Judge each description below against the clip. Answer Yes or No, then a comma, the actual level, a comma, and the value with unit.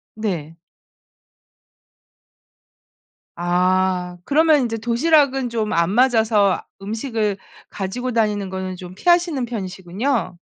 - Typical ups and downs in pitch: Yes, average, 5.0 semitones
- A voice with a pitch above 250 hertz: No, high, 215 Hz